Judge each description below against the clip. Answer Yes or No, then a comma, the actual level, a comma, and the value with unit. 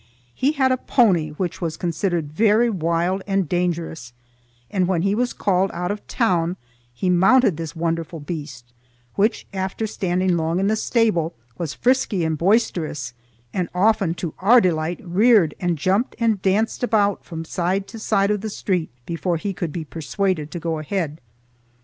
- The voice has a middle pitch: Yes, medium, 180 Hz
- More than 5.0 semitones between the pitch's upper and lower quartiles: No, average, 3.8 semitones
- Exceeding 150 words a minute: Yes, average, 170 wpm